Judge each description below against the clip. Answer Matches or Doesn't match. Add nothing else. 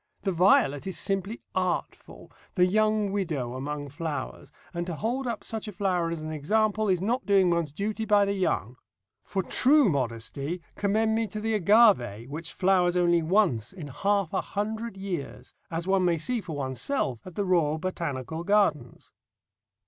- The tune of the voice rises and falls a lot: Doesn't match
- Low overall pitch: Doesn't match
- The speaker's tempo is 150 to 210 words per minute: Matches